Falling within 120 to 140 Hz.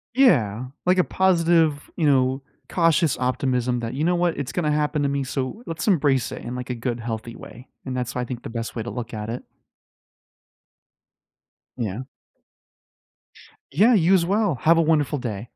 Yes: low, 135 Hz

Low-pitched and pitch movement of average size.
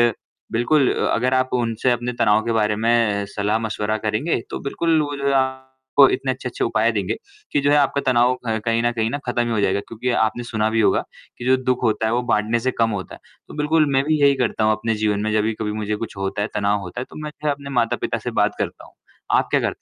Yes: low, 115 Hz; average, 3.4 semitones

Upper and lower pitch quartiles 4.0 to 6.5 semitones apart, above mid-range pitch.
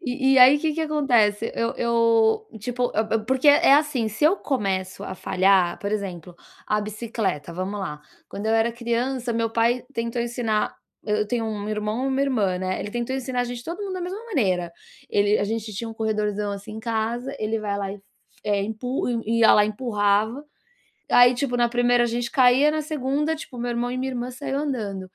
No: average, 3.3 semitones; high, 230 Hz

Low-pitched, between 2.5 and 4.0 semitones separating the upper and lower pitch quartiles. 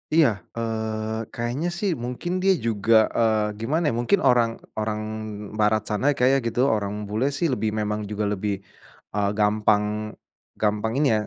Yes: low, 110 Hz; average, 2.8 semitones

